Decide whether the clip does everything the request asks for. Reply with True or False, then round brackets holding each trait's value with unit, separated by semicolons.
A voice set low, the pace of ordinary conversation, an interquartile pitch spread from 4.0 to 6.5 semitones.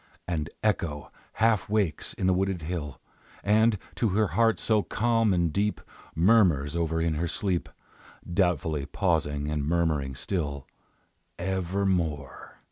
False (85 Hz; 125 wpm; 4.6 semitones)